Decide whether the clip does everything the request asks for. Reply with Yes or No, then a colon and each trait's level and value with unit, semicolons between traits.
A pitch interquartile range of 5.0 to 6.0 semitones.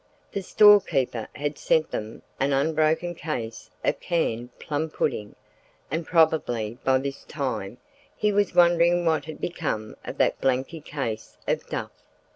Yes: wide, 5.4 semitones